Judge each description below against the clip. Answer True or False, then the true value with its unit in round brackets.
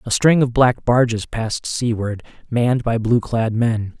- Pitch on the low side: True (115 Hz)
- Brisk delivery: False (180 wpm)